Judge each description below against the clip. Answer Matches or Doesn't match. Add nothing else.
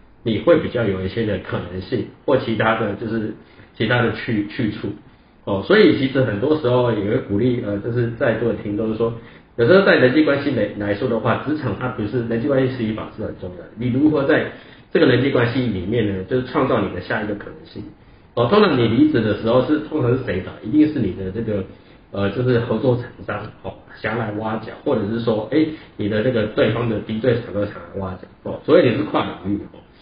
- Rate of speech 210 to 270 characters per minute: Doesn't match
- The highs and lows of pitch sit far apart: Doesn't match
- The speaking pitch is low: Matches